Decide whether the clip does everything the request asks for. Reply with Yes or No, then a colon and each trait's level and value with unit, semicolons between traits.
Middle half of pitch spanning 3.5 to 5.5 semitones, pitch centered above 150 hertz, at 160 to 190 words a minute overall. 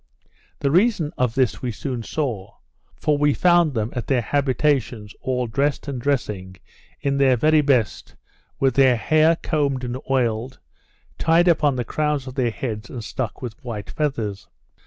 No: average, 3.8 semitones; low, 130 Hz; average, 165 wpm